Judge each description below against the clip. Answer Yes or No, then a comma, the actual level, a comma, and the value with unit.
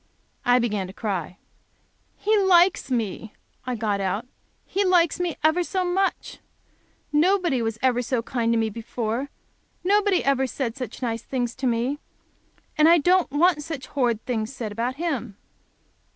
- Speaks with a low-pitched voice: No, very high, 260 Hz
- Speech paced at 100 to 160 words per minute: Yes, average, 155 wpm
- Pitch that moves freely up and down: Yes, wide, 6.9 semitones